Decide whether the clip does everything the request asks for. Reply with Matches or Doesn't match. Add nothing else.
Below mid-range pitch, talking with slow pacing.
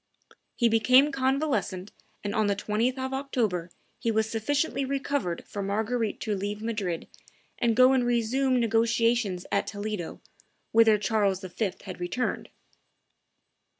Doesn't match